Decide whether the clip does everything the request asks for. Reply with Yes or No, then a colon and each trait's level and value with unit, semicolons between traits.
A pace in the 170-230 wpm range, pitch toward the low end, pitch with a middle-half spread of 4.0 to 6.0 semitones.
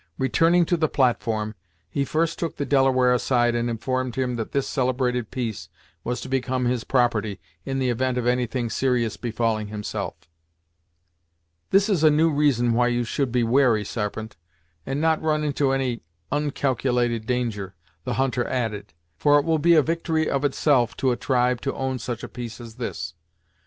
No: average, 175 wpm; low, 125 Hz; average, 2.9 semitones